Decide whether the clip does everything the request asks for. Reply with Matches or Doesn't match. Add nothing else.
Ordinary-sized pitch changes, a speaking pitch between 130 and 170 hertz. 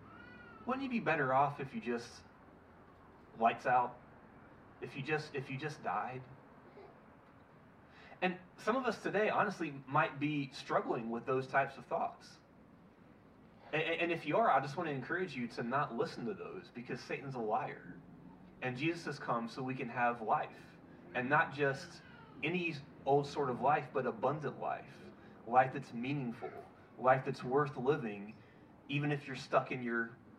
Matches